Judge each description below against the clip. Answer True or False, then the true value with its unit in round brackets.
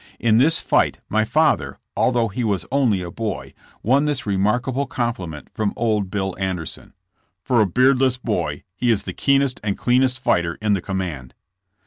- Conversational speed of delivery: True (165 wpm)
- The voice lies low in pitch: True (110 Hz)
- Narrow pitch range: False (5.0 semitones)